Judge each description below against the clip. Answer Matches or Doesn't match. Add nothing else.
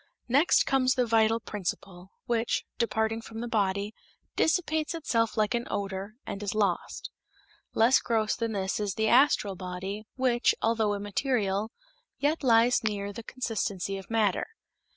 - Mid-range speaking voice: Doesn't match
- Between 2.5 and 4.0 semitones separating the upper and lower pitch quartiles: Matches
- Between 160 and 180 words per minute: Doesn't match